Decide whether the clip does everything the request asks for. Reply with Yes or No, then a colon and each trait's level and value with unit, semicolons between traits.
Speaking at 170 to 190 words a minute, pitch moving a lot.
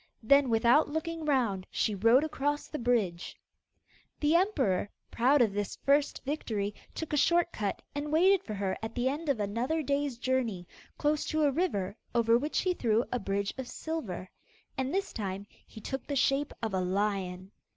Yes: average, 180 wpm; wide, 6.3 semitones